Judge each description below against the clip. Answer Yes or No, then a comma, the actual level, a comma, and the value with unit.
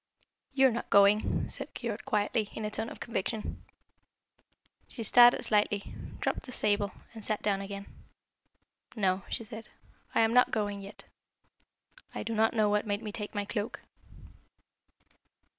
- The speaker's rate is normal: Yes, average, 155 wpm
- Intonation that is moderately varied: No, narrow, 1.8 semitones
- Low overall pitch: No, high, 210 Hz